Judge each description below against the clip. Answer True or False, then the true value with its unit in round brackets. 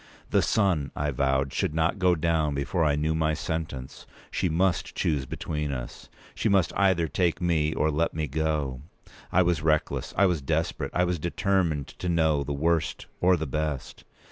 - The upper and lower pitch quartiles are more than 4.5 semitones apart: False (2.9 semitones)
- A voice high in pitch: False (80 Hz)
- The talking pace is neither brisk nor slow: True (180 wpm)